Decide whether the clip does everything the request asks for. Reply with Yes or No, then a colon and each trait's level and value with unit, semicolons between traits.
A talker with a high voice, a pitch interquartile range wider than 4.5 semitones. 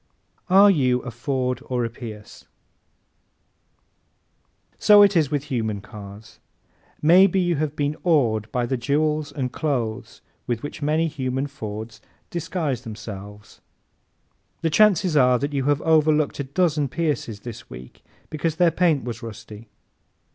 No: medium, 140 Hz; average, 5.1 semitones